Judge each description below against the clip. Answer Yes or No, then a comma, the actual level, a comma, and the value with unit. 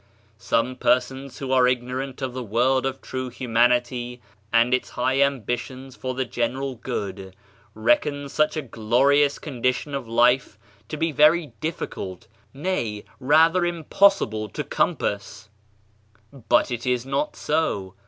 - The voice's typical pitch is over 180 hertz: No, low, 130 Hz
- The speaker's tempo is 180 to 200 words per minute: No, slow, 135 wpm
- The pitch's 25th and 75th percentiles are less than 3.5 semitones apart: Yes, average, 2.8 semitones